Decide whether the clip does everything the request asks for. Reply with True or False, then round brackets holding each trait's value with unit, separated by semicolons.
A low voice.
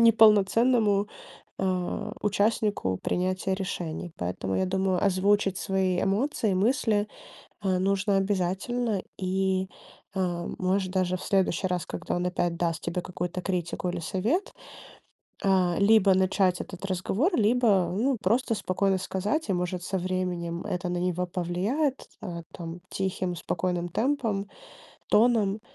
False (190 Hz)